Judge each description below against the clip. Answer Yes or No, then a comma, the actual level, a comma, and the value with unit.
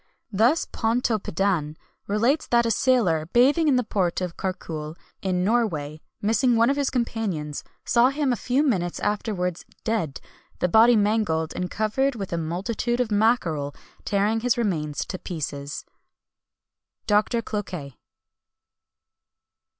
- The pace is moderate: No, slow, 130 wpm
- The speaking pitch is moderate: No, high, 210 Hz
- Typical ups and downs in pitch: No, wide, 5.7 semitones